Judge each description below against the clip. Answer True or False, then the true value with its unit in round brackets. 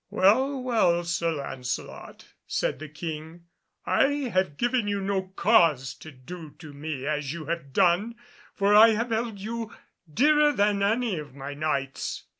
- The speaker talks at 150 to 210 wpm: True (155 wpm)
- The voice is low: False (180 Hz)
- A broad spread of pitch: True (6.6 semitones)